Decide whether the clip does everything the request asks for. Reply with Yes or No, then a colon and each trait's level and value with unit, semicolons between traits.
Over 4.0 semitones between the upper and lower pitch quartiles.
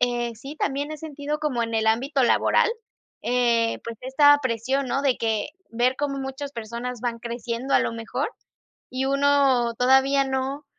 No: average, 2.9 semitones